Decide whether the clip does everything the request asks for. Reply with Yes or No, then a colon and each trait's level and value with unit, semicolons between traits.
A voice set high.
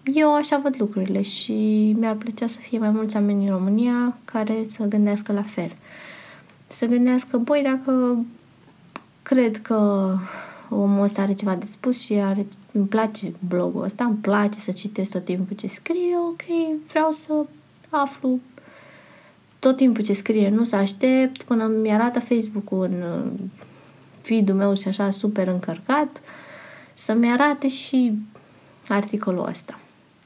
Yes: high, 220 Hz